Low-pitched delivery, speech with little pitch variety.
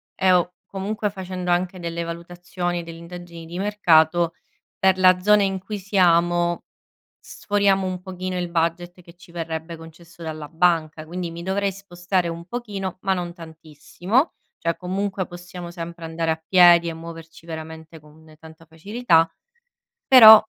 No: medium, 175 Hz; narrow, 2.2 semitones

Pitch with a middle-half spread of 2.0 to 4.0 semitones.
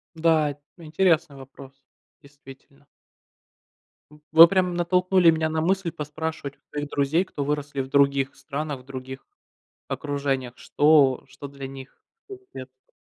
Yes: average, 2.9 semitones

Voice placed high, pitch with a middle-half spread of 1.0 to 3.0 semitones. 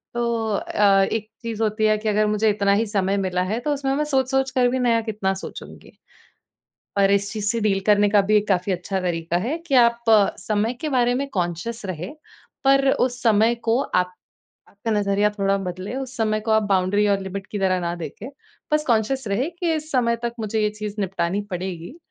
No: high, 210 Hz; average, 3.4 semitones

